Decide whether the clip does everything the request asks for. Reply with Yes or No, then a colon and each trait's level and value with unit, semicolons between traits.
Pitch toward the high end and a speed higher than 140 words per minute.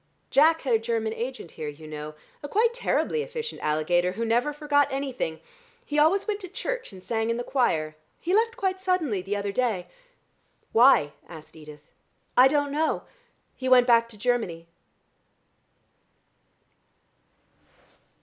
Yes: high, 245 Hz; average, 150 wpm